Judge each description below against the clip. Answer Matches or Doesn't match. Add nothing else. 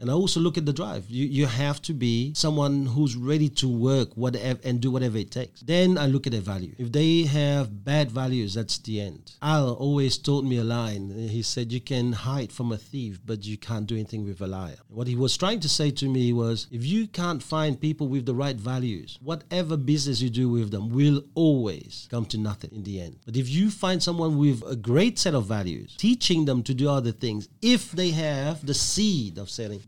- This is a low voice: Matches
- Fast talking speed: Matches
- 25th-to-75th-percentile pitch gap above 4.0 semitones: Matches